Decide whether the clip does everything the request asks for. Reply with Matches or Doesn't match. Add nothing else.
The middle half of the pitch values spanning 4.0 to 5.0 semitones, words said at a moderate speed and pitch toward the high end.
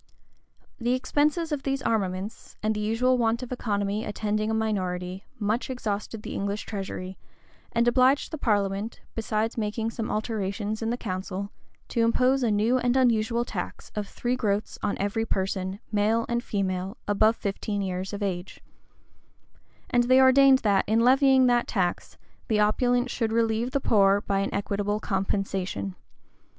Doesn't match